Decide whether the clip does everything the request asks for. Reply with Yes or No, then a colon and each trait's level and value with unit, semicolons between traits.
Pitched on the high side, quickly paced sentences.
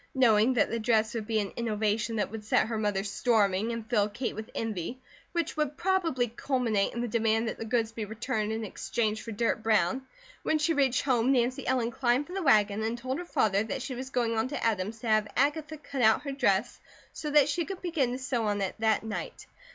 Yes: high, 230 Hz; fast, 230 wpm